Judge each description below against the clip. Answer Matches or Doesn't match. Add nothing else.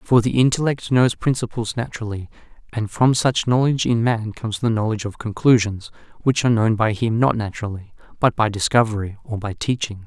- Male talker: Matches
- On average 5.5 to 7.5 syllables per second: Matches